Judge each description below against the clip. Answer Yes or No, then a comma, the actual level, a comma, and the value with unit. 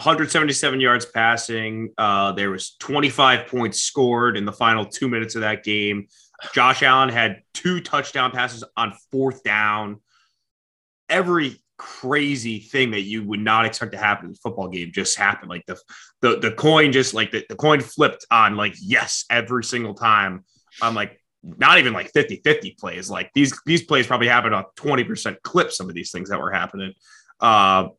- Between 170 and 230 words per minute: Yes, average, 180 wpm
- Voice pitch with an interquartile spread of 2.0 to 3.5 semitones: No, average, 4.1 semitones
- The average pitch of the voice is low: Yes, low, 115 Hz